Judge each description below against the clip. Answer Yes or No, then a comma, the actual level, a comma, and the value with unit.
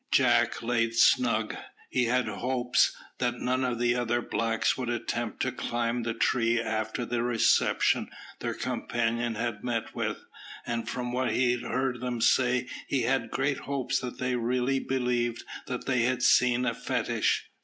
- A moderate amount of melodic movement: No, narrow, 1.4 semitones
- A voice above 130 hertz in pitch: No, low, 120 Hz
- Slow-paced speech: No, average, 155 wpm